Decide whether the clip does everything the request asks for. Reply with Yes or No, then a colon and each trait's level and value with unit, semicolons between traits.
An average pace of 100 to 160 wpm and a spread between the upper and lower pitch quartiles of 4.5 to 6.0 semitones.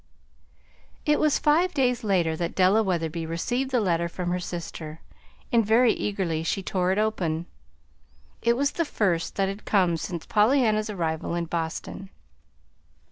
Yes: average, 150 wpm; average, 5.1 semitones